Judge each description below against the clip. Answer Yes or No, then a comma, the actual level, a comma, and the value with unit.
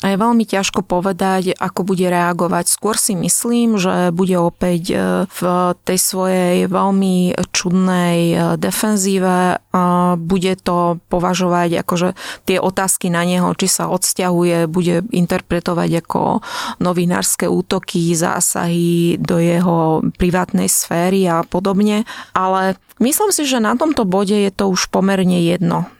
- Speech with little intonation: Yes, narrow, 1.8 semitones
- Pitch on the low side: No, medium, 180 Hz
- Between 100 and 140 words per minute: Yes, average, 130 wpm